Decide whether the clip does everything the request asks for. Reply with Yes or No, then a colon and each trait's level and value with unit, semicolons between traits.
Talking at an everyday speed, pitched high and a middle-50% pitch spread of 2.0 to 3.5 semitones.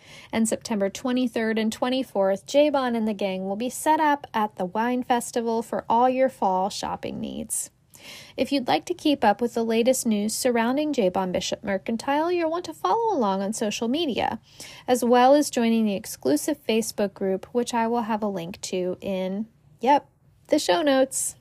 No: average, 180 wpm; high, 235 Hz; average, 4.4 semitones